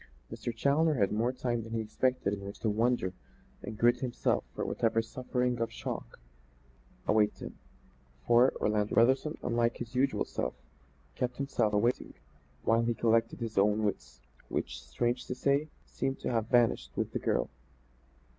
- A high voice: No, low, 115 Hz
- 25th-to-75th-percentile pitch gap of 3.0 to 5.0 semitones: No, narrow, 2.6 semitones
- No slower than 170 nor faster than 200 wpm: No, average, 160 wpm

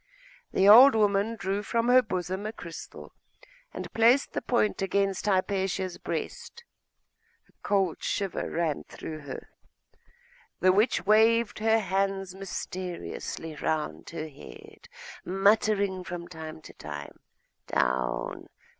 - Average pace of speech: No, slow, 120 wpm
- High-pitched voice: Yes, high, 195 Hz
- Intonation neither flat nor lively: Yes, average, 3.6 semitones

